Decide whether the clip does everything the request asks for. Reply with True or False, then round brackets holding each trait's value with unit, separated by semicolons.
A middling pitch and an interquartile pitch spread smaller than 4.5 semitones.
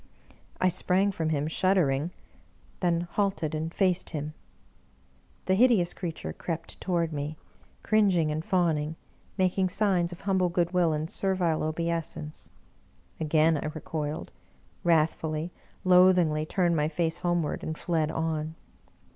True (165 Hz; 2.7 semitones)